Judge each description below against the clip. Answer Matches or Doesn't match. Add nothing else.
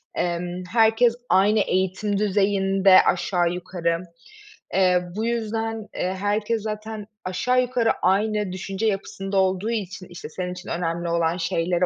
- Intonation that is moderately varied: Matches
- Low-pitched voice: Doesn't match